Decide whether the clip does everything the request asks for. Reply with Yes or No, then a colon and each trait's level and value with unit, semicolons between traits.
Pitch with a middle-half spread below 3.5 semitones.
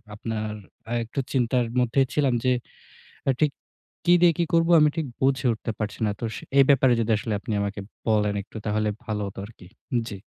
No: average, 4.2 semitones